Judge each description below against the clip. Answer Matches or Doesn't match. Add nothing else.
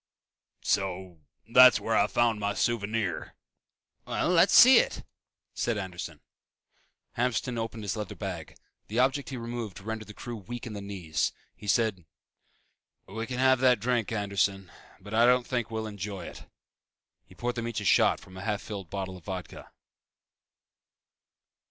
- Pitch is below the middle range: Matches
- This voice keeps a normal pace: Matches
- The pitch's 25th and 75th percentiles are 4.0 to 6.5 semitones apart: Doesn't match